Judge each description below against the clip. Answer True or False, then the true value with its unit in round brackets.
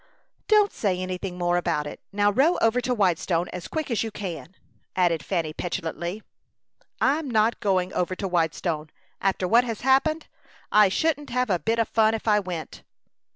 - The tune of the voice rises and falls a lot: False (4.8 semitones)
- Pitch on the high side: True (195 Hz)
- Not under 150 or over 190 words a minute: True (175 wpm)